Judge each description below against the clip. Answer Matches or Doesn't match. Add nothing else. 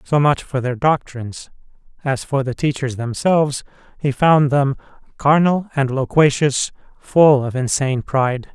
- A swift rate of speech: Doesn't match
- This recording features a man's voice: Matches